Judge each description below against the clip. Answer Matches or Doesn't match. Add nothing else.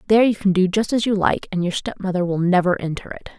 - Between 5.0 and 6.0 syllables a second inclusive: Doesn't match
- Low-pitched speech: Doesn't match